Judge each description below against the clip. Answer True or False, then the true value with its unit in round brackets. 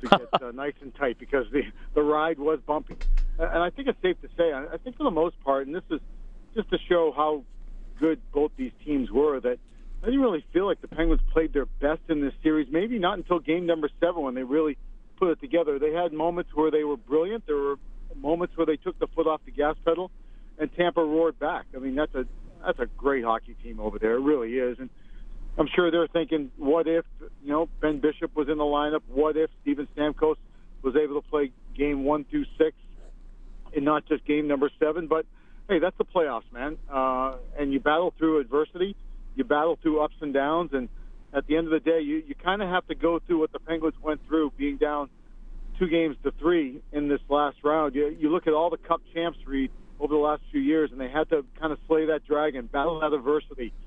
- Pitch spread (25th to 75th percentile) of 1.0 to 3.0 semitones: True (2.6 semitones)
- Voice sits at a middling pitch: True (155 Hz)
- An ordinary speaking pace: False (230 wpm)